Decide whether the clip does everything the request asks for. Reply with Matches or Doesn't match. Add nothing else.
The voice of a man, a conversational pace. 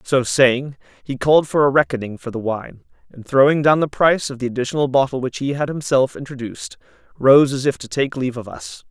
Doesn't match